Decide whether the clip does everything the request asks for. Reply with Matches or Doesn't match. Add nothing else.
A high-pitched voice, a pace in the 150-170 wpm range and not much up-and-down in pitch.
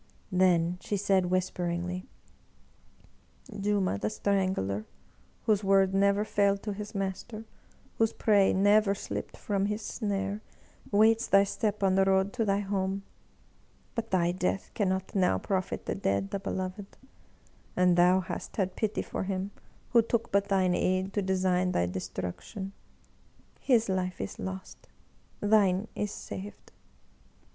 Doesn't match